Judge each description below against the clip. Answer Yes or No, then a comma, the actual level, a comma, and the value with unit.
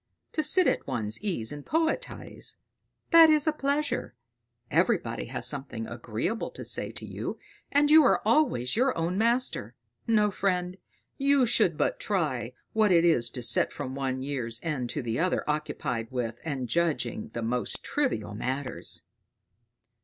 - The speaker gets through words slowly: No, average, 155 wpm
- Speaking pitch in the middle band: Yes, medium, 160 Hz